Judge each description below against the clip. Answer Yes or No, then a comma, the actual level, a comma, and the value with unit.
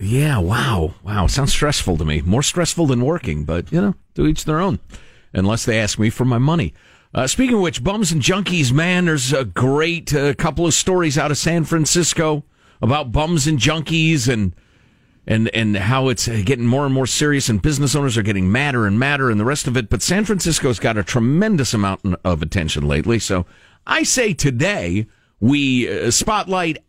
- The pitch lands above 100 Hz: Yes, low, 135 Hz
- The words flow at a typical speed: Yes, average, 195 wpm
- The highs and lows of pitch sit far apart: Yes, wide, 6.5 semitones